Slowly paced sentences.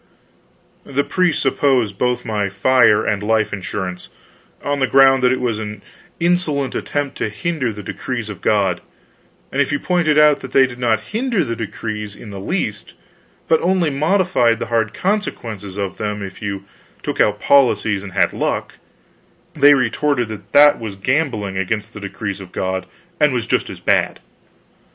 No: average, 170 wpm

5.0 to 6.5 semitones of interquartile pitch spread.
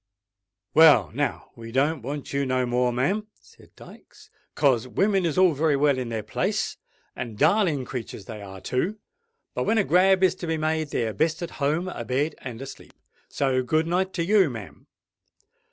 Yes: wide, 5.4 semitones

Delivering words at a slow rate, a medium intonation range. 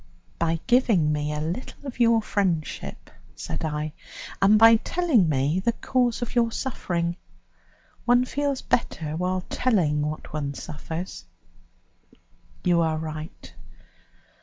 No: slow, 125 wpm; wide, 7.2 semitones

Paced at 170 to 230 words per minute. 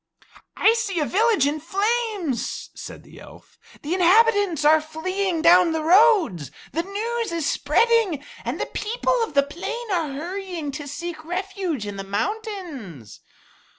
No: average, 150 wpm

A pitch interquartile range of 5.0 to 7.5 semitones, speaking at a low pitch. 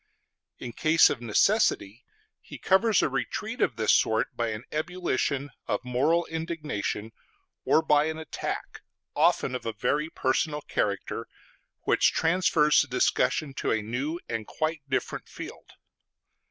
No: average, 5.3 semitones; medium, 145 Hz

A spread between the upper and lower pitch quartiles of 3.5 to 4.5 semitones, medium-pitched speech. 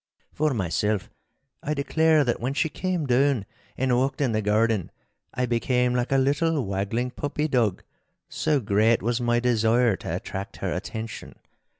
No: average, 4.0 semitones; low, 125 Hz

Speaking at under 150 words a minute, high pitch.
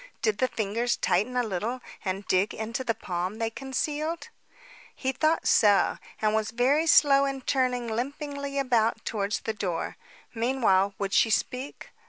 No: average, 155 wpm; high, 235 Hz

